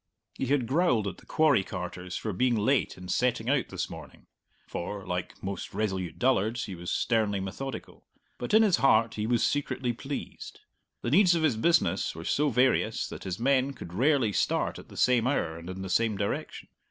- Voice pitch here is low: Yes, low, 115 Hz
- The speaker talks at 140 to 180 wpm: No, average, 195 wpm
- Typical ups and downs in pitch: No, wide, 6.0 semitones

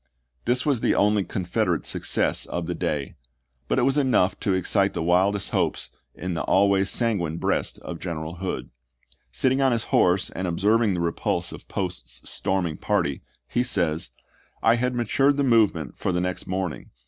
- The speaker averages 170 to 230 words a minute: Yes, average, 185 wpm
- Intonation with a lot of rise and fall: No, average, 5.0 semitones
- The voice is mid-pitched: No, very low, 95 Hz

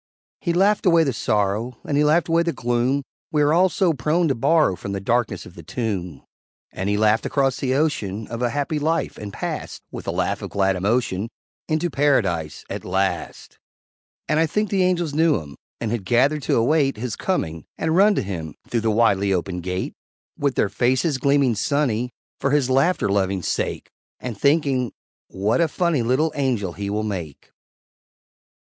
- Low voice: Yes, low, 125 Hz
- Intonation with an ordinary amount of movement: No, wide, 7.2 semitones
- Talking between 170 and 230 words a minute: Yes, average, 185 wpm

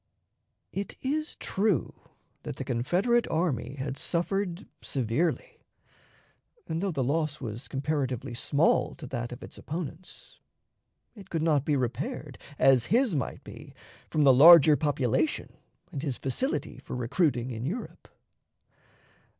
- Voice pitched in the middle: Yes, medium, 145 Hz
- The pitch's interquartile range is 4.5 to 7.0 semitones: Yes, average, 5.2 semitones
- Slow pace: Yes, slow, 130 wpm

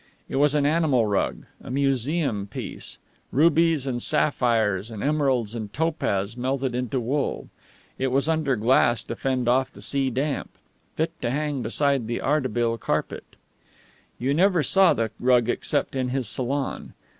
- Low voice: Yes, low, 130 Hz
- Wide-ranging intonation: No, average, 3.5 semitones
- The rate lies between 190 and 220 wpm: No, average, 155 wpm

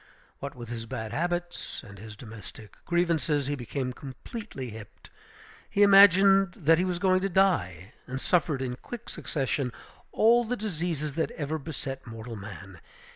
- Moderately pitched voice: Yes, medium, 145 Hz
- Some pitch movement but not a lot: No, wide, 7.2 semitones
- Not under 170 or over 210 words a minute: No, average, 155 wpm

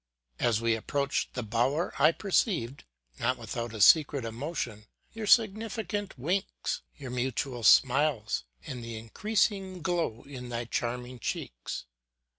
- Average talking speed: No, slow, 125 wpm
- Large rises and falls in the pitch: Yes, wide, 6.8 semitones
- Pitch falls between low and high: No, low, 130 Hz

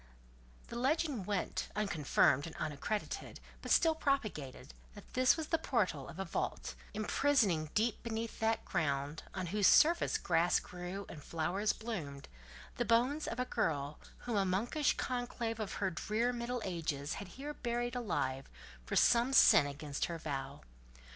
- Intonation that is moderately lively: No, wide, 7.2 semitones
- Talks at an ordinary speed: Yes, average, 155 wpm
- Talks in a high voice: Yes, high, 205 Hz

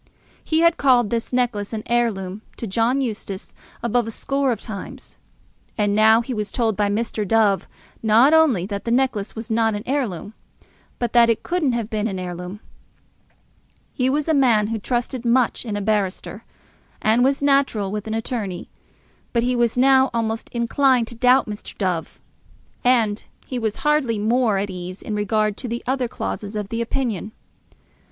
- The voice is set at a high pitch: Yes, high, 225 Hz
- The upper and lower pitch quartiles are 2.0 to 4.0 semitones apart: Yes, average, 3.3 semitones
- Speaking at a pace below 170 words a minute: No, average, 175 wpm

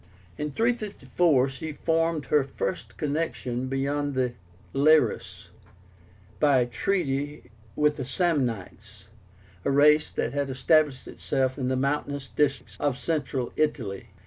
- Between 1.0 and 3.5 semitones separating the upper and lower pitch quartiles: Yes, average, 2.8 semitones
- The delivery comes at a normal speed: No, slow, 120 wpm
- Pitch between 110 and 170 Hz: Yes, medium, 140 Hz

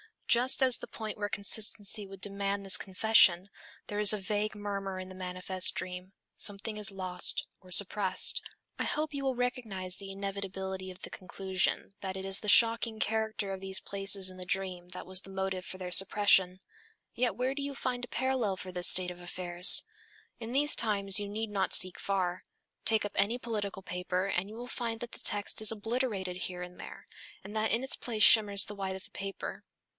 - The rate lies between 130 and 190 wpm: No, average, 200 wpm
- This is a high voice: Yes, high, 200 Hz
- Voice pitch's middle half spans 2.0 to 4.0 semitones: Yes, average, 2.7 semitones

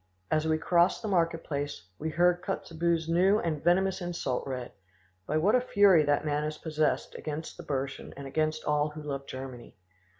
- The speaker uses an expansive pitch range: No, average, 3.0 semitones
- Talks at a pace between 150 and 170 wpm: No, average, 180 wpm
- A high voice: No, medium, 155 Hz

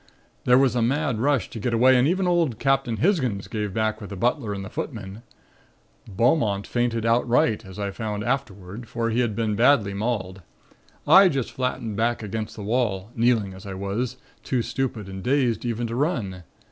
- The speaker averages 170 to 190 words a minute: Yes, average, 185 wpm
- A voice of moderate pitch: No, low, 115 Hz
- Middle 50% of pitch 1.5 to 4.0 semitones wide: Yes, average, 3.7 semitones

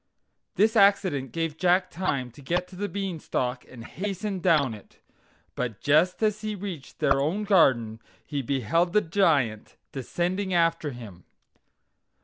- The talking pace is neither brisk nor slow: Yes, average, 145 wpm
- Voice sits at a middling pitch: Yes, medium, 165 Hz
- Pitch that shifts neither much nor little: No, wide, 6.4 semitones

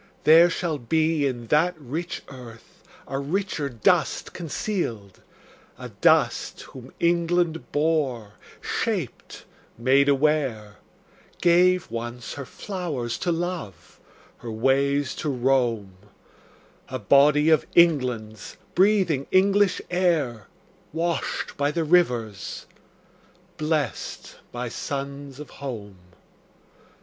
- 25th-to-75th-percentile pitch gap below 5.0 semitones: No, wide, 5.6 semitones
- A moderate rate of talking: No, slow, 100 wpm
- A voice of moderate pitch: Yes, medium, 145 Hz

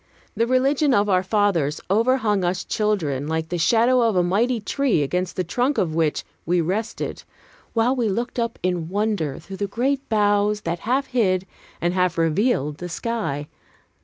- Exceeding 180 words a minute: No, average, 170 wpm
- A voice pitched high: Yes, high, 205 Hz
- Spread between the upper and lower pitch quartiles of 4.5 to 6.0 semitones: Yes, average, 5.0 semitones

